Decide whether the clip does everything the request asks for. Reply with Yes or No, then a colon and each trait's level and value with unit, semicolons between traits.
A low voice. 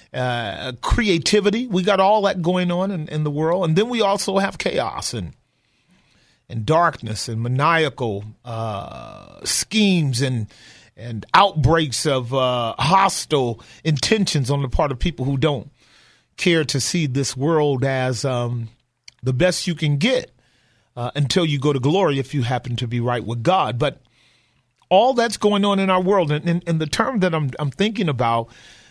No: medium, 145 Hz